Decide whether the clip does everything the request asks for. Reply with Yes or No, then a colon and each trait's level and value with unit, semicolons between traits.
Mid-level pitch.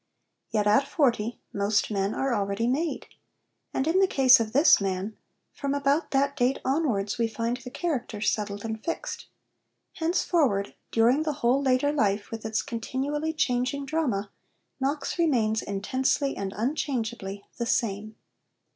No: high, 245 Hz